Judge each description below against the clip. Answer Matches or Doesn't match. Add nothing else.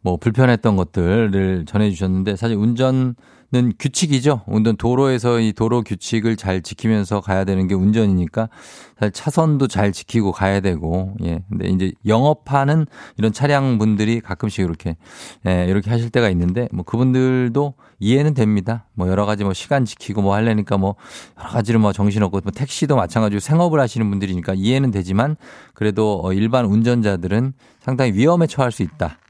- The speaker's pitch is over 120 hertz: Doesn't match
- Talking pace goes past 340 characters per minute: Matches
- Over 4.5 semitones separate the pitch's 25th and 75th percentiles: Doesn't match